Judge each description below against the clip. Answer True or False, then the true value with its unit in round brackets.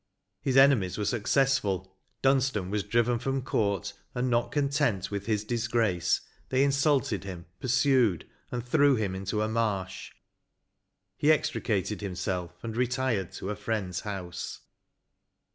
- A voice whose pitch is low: True (110 Hz)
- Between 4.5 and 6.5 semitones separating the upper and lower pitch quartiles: True (5.0 semitones)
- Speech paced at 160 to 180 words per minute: False (135 wpm)